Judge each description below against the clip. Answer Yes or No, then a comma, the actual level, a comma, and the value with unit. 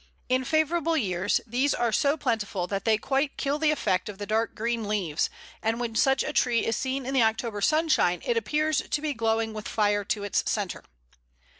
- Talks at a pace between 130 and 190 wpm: No, average, 200 wpm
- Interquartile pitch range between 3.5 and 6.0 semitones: Yes, average, 4.7 semitones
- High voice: Yes, high, 230 Hz